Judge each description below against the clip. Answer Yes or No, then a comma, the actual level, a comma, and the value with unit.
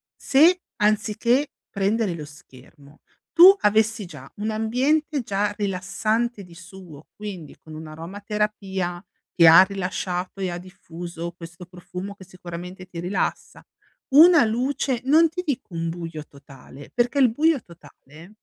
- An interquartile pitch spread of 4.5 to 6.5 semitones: Yes, average, 4.8 semitones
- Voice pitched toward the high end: Yes, high, 195 Hz